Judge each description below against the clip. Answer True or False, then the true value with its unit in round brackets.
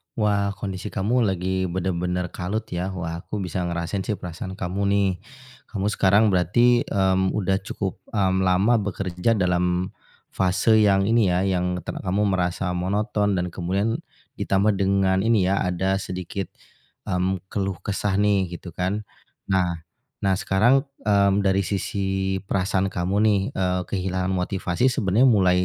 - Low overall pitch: True (95 Hz)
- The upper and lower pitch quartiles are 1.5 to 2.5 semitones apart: True (1.8 semitones)